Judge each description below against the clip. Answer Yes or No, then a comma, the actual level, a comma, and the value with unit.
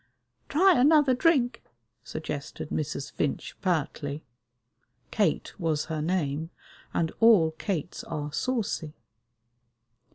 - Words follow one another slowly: Yes, slow, 95 wpm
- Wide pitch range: Yes, wide, 7.9 semitones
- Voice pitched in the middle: Yes, medium, 165 Hz